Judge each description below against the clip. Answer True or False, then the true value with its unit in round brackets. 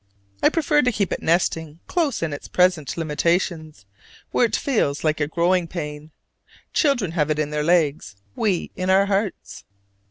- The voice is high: False (170 Hz)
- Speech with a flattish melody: False (4.5 semitones)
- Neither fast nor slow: True (165 wpm)